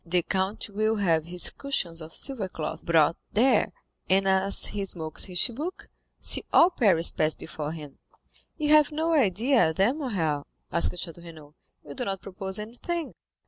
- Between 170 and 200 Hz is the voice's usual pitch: Yes, high, 190 Hz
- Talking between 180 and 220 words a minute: No, average, 165 wpm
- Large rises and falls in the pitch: Yes, wide, 6.2 semitones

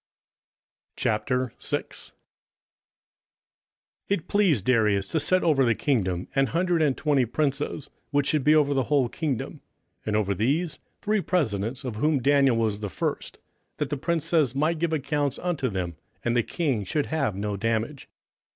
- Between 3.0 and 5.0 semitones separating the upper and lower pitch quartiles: No, wide, 5.5 semitones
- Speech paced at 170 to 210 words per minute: No, average, 150 wpm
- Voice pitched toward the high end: No, low, 135 Hz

